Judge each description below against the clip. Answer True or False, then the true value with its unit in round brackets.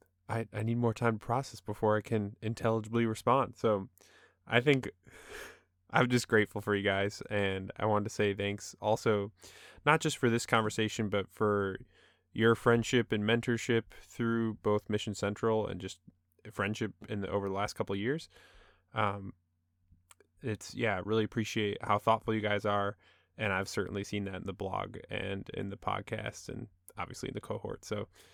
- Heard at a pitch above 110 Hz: False (105 Hz)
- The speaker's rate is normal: True (175 wpm)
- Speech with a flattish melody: True (2.3 semitones)